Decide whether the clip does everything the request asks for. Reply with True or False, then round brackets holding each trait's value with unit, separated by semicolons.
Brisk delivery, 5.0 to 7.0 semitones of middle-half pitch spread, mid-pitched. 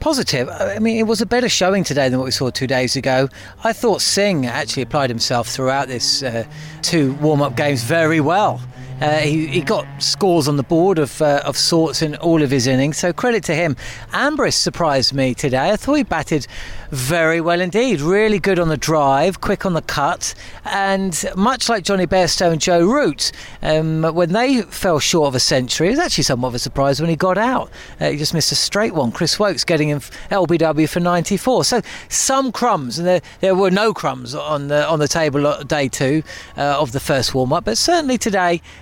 True (210 wpm; 5.5 semitones; 155 Hz)